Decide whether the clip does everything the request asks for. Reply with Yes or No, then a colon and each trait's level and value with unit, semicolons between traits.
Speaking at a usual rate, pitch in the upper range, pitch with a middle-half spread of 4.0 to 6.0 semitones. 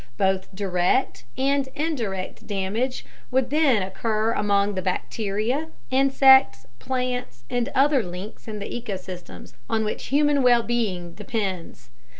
No: slow, 125 wpm; high, 220 Hz; wide, 5.5 semitones